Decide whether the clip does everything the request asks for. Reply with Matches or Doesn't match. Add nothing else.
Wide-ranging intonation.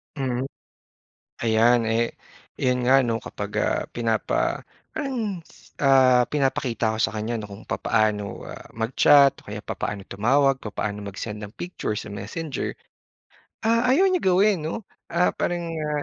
Matches